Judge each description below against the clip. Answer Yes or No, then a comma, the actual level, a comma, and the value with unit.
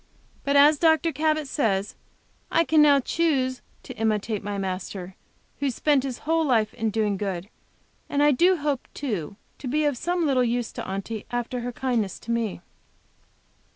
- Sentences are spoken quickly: No, average, 170 wpm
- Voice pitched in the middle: No, very high, 250 Hz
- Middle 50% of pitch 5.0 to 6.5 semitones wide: Yes, wide, 5.5 semitones